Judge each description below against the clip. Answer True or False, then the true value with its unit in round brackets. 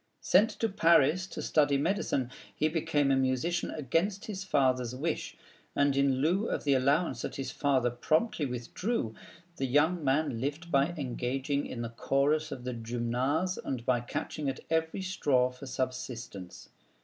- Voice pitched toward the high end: False (140 Hz)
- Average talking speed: True (160 wpm)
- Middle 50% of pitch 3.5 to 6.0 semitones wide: True (4.1 semitones)